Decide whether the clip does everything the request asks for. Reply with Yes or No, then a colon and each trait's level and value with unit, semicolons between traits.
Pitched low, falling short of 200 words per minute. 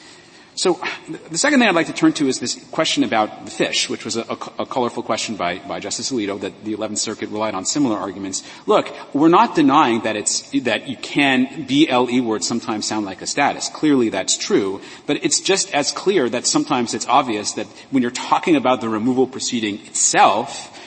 No: low, 125 Hz; fast, 205 wpm